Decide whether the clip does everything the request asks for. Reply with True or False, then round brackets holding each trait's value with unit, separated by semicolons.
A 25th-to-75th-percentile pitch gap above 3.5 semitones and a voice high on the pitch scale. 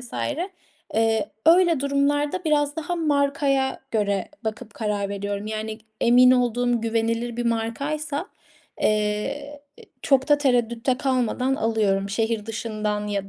True (4.5 semitones; 235 Hz)